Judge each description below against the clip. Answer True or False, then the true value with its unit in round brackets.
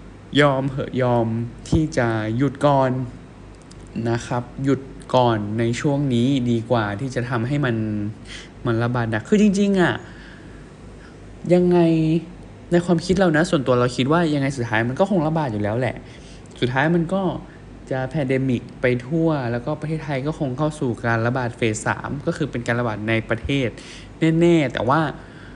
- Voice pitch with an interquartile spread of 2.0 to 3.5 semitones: False (4.8 semitones)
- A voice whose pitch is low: True (130 Hz)